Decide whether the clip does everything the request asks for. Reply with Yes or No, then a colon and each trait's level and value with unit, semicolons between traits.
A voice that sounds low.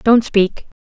No: high, 215 Hz